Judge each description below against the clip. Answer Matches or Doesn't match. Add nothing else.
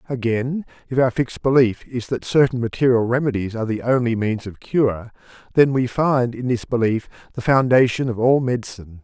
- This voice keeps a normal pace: Matches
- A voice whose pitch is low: Matches